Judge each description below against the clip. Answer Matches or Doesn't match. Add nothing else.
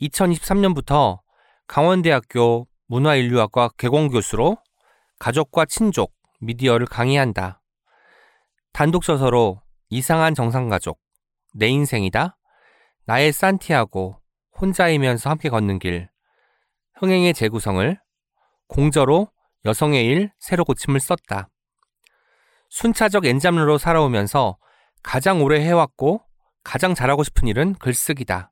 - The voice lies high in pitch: Doesn't match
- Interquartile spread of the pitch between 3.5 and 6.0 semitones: Doesn't match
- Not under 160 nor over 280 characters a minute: Matches